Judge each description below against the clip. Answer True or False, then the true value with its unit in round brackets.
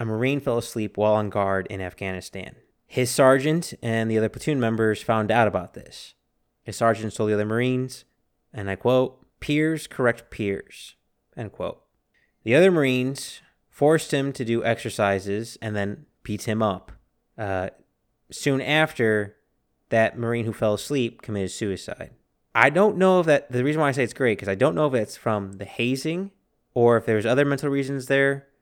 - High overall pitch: False (115 Hz)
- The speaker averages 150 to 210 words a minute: True (180 wpm)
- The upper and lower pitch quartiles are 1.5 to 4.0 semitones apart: False (4.5 semitones)